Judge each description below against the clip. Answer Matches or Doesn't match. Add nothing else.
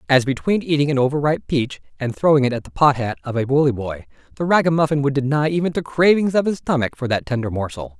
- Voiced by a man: Matches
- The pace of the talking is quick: Matches